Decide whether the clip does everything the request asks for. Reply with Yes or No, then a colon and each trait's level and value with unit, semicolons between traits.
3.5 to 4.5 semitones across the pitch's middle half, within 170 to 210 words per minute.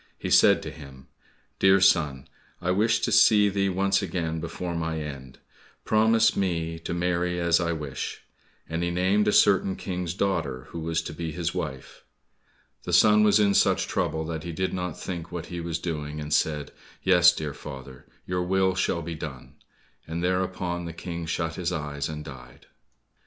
No: average, 2.9 semitones; average, 180 wpm